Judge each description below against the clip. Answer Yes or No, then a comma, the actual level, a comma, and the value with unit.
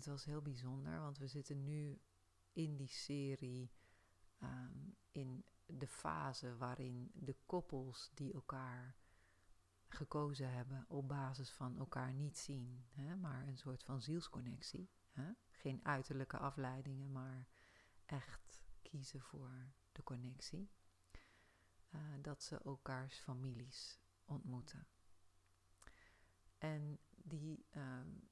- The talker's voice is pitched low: Yes, low, 130 Hz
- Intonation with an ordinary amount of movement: No, wide, 7.0 semitones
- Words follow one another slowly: Yes, slow, 110 wpm